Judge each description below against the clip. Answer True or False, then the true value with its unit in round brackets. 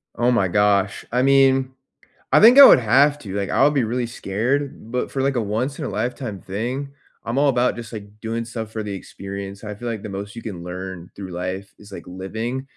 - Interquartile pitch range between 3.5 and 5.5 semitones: True (4.3 semitones)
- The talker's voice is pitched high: False (110 Hz)